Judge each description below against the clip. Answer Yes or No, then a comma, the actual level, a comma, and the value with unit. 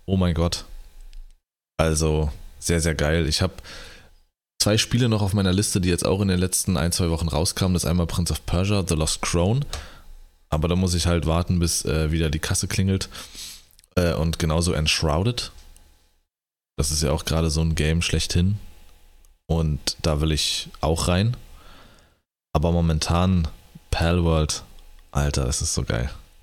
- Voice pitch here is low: Yes, very low, 80 Hz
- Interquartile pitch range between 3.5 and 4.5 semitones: No, average, 2.9 semitones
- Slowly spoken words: No, average, 170 wpm